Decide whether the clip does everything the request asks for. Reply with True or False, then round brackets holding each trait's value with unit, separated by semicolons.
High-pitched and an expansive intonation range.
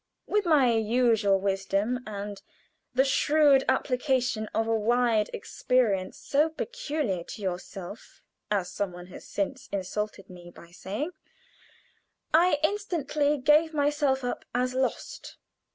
True (245 Hz; 6.3 semitones)